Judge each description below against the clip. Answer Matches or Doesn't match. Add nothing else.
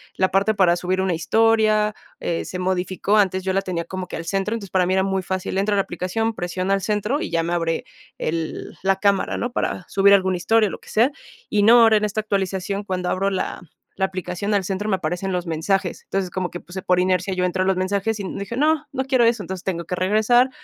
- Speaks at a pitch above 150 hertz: Matches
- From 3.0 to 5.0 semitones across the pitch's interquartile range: Doesn't match